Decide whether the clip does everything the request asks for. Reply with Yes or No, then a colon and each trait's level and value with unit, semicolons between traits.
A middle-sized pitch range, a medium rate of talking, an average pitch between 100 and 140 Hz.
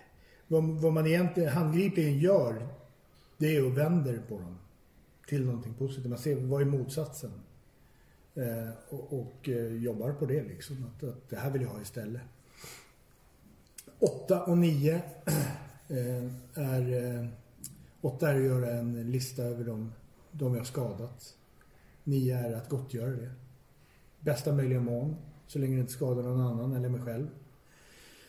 Yes: average, 3.4 semitones; average, 145 wpm; low, 130 Hz